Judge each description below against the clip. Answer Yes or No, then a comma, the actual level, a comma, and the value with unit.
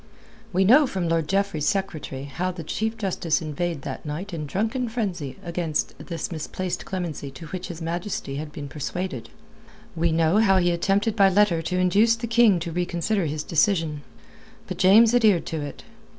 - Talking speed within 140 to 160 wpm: No, average, 175 wpm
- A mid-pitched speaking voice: Yes, medium, 175 Hz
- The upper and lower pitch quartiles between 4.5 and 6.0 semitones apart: No, average, 4.0 semitones